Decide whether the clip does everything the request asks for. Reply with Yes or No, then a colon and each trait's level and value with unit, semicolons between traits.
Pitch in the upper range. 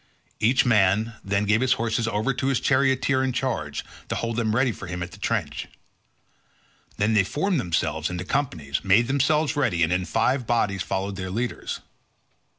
No: low, 110 Hz